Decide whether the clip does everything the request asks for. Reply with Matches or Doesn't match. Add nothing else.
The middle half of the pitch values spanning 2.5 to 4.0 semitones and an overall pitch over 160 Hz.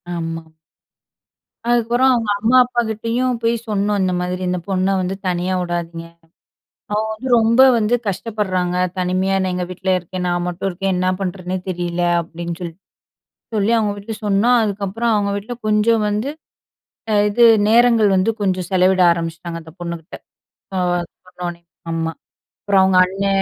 Matches